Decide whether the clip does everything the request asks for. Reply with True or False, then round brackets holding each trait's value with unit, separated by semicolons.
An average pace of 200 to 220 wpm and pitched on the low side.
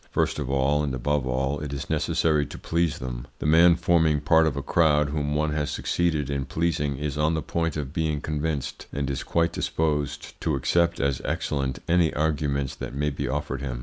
True (205 wpm; 75 Hz)